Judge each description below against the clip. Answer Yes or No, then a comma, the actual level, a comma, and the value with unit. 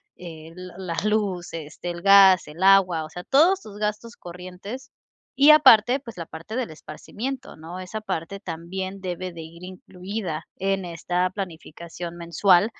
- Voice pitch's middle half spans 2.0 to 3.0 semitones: No, average, 3.6 semitones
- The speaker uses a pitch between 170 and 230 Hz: Yes, medium, 185 Hz